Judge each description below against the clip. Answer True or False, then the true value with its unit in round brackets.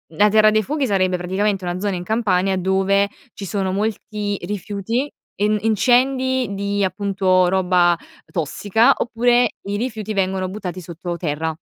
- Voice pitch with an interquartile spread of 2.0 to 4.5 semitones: True (2.7 semitones)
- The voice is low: False (200 Hz)